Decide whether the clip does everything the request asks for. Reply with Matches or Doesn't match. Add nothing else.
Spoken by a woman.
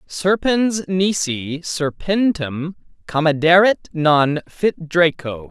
Doesn't match